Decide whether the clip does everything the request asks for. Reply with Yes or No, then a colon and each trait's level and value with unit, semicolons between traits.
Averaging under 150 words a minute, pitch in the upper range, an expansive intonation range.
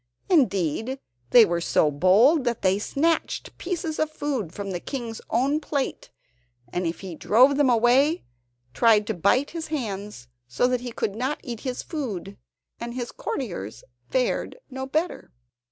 No: average, 155 wpm; high, 240 Hz; wide, 6.0 semitones